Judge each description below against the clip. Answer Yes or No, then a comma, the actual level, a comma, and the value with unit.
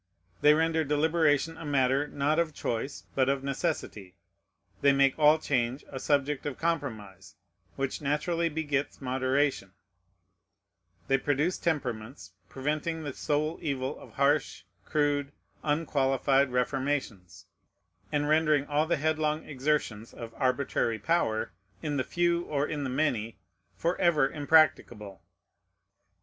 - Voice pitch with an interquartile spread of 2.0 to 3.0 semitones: Yes, average, 2.7 semitones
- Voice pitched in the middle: Yes, medium, 145 Hz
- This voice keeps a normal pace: No, slow, 120 wpm